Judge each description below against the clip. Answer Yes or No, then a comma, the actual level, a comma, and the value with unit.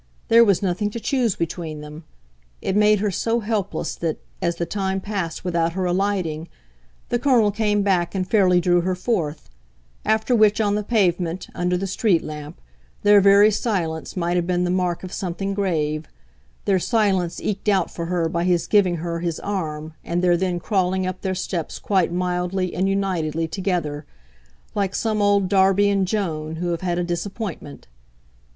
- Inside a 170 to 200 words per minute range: Yes, average, 175 wpm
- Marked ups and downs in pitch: No, average, 3.0 semitones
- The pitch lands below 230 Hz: Yes, medium, 185 Hz